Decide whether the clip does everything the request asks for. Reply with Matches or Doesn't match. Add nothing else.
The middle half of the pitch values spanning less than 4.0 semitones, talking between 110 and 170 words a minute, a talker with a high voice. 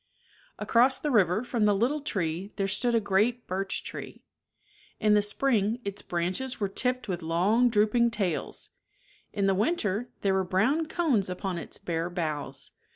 Doesn't match